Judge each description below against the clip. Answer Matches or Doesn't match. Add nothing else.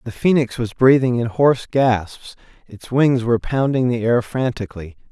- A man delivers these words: Matches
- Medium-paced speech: Matches